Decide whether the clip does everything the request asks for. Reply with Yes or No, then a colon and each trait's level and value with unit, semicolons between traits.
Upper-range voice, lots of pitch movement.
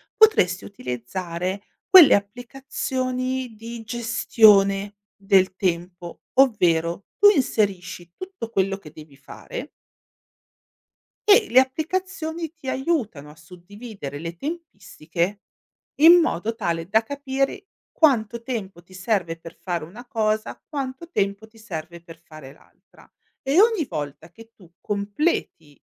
Yes: high, 210 Hz; wide, 7.2 semitones